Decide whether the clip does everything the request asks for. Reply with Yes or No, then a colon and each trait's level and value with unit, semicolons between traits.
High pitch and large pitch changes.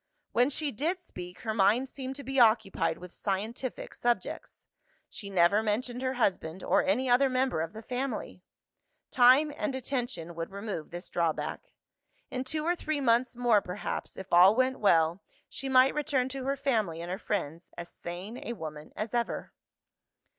Yes: high, 235 Hz; wide, 6.0 semitones